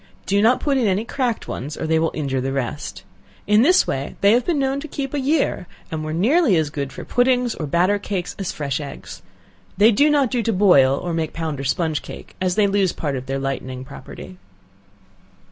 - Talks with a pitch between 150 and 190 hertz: Yes, medium, 185 Hz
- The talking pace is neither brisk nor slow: No, fast, 220 wpm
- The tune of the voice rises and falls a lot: Yes, wide, 8.9 semitones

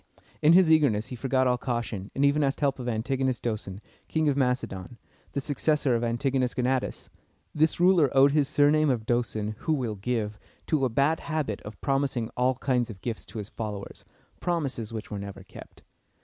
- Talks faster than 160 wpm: Yes, average, 185 wpm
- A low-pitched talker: Yes, low, 125 Hz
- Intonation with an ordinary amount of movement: Yes, average, 4.1 semitones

